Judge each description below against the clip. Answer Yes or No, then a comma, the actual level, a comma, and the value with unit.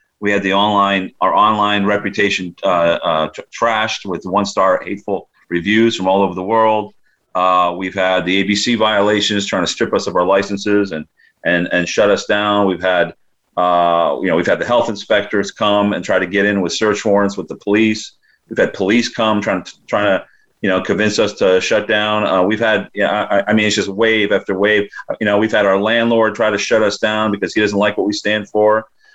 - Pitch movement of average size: No, narrow, 1.7 semitones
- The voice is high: No, low, 105 Hz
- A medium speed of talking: No, fast, 220 wpm